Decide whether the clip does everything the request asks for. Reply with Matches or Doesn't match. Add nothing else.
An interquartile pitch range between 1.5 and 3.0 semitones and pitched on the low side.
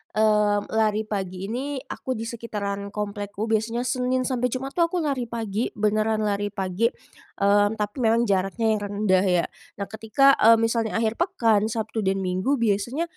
Doesn't match